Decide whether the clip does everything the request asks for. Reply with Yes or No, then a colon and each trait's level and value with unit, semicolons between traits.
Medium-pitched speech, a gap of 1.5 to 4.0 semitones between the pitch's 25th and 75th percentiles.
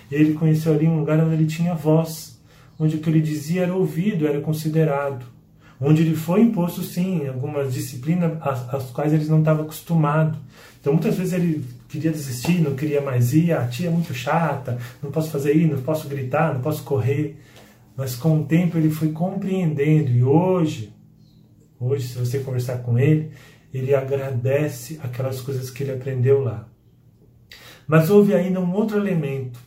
Yes: medium, 150 Hz; average, 3.1 semitones